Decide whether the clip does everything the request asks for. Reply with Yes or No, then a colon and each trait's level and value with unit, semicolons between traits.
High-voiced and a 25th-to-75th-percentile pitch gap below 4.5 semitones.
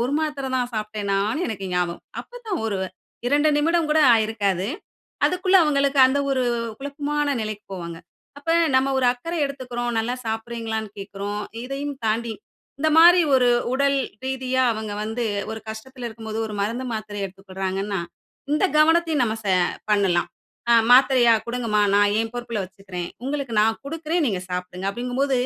No: high, 235 Hz; average, 5.1 semitones